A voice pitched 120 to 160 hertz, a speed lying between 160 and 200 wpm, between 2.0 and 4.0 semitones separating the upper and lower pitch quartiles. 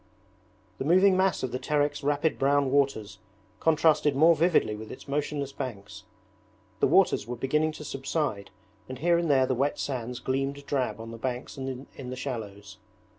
Yes: low, 135 Hz; average, 175 wpm; average, 3.3 semitones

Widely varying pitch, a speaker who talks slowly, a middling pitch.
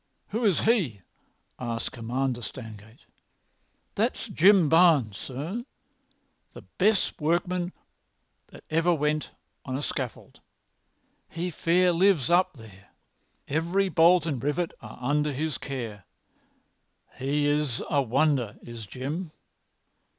Yes: wide, 5.7 semitones; slow, 110 wpm; medium, 150 Hz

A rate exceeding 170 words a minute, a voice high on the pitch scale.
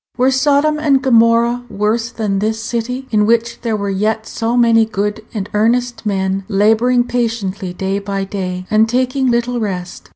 No: average, 165 wpm; high, 225 Hz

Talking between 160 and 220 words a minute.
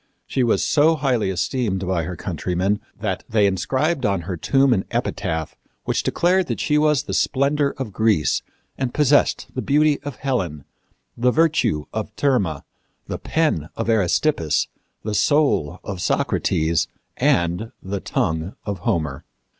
No: average, 145 wpm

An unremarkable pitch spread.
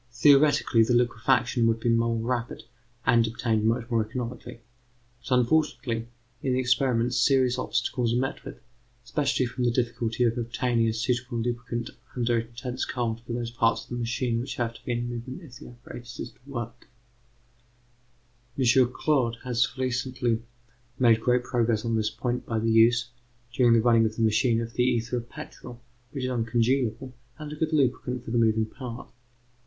No: narrow, 1.5 semitones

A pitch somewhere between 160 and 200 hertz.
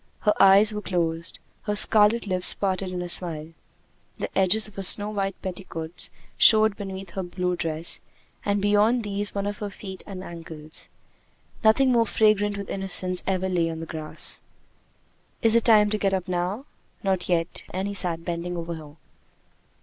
Yes: high, 190 Hz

